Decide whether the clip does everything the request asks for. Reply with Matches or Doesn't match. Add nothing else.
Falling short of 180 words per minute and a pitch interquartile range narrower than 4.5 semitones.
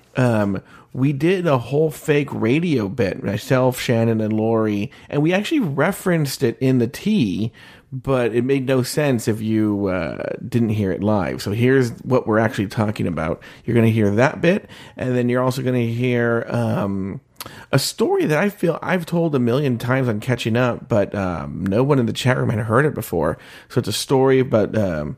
Doesn't match